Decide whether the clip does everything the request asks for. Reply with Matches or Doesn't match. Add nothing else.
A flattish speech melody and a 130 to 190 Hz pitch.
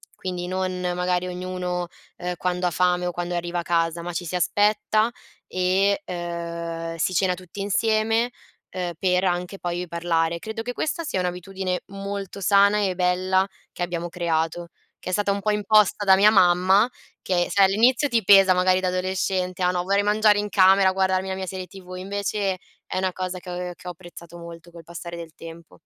Matches